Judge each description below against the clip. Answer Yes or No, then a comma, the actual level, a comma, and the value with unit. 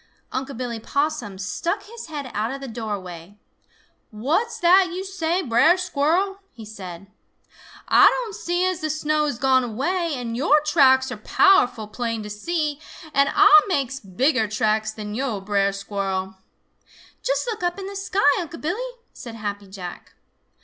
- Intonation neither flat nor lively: No, wide, 8.3 semitones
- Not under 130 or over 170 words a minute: Yes, average, 160 wpm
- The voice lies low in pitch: No, very high, 270 Hz